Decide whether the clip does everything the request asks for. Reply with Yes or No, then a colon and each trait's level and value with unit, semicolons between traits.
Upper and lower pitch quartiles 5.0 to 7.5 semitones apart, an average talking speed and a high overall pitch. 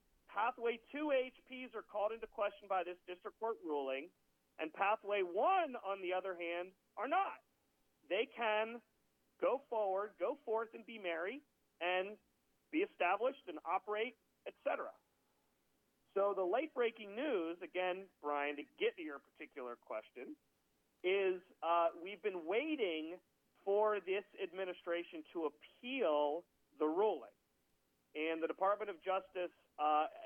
No: wide, 5.4 semitones; slow, 130 wpm; high, 195 Hz